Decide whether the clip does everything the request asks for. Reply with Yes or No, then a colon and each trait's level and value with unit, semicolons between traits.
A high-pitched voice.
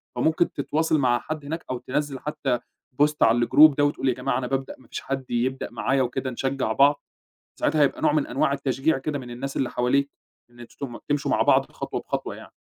No: low, 135 Hz